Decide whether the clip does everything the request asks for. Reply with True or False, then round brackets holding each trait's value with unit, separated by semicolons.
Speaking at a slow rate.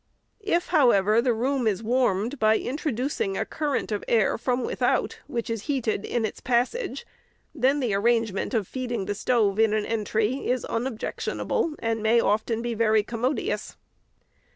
False (155 wpm)